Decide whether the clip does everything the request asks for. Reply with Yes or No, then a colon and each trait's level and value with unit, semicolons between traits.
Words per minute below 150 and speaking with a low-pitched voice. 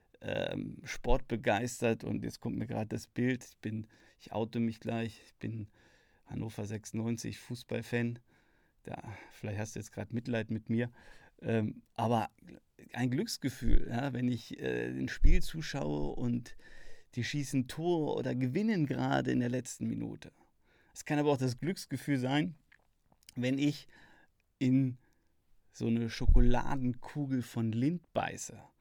Yes: average, 135 wpm; low, 120 Hz